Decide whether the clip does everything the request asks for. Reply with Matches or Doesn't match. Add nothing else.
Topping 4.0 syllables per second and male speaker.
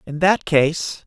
Matches